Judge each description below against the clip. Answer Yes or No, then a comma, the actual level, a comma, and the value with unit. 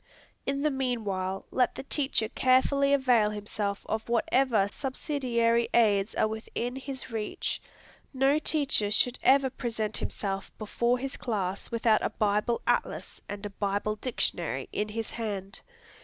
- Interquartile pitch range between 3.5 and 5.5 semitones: Yes, average, 3.9 semitones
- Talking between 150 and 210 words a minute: No, average, 140 wpm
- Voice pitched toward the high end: Yes, high, 230 Hz